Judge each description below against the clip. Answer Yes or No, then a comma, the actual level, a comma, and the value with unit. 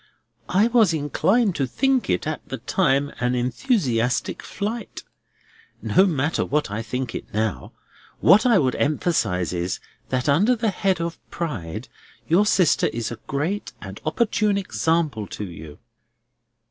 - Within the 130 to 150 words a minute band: Yes, average, 145 wpm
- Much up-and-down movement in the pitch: Yes, wide, 8.6 semitones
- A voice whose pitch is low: No, medium, 150 Hz